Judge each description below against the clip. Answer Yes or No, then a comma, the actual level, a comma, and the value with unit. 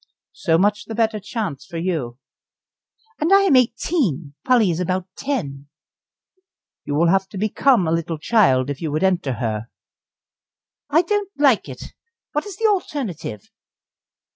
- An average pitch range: No, wide, 9.0 semitones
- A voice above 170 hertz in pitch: Yes, high, 190 Hz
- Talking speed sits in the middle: Yes, average, 150 wpm